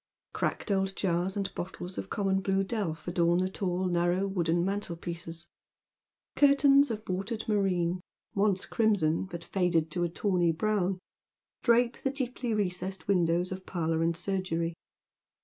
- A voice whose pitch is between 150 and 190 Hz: Yes, medium, 185 Hz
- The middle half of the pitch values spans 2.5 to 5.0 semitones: Yes, average, 2.8 semitones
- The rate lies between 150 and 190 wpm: No, average, 140 wpm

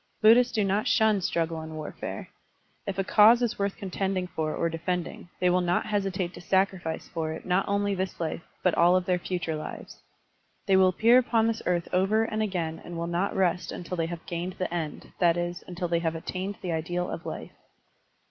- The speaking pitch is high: No, medium, 180 Hz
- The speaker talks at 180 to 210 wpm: Yes, fast, 205 wpm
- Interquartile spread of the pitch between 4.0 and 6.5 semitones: No, narrow, 2.6 semitones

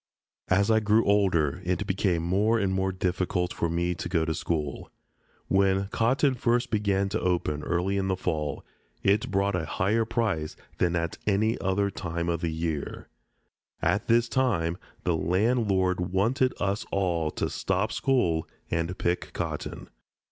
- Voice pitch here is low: Yes, very low, 95 Hz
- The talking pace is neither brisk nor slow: Yes, average, 155 wpm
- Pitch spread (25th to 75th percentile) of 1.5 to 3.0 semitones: No, average, 3.4 semitones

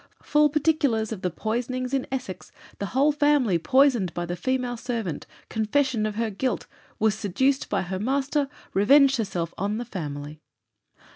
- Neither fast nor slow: Yes, average, 155 wpm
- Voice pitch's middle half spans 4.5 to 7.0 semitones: Yes, wide, 5.5 semitones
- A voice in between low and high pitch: No, high, 230 Hz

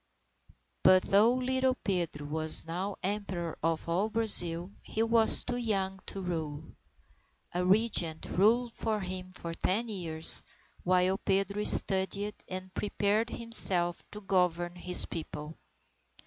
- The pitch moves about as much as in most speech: Yes, average, 3.4 semitones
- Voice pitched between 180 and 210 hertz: Yes, high, 190 Hz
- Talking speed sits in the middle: No, slow, 125 wpm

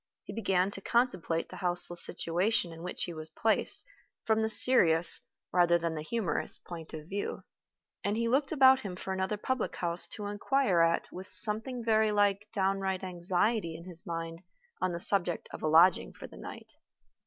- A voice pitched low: No, high, 190 Hz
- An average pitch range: Yes, average, 4.1 semitones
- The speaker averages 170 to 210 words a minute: Yes, average, 180 wpm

